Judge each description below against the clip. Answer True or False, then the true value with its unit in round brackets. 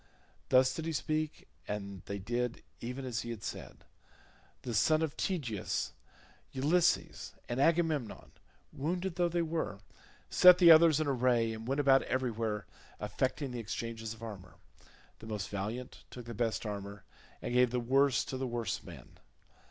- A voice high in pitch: False (125 Hz)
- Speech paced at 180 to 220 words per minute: False (160 wpm)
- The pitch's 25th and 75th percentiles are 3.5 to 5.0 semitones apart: False (5.4 semitones)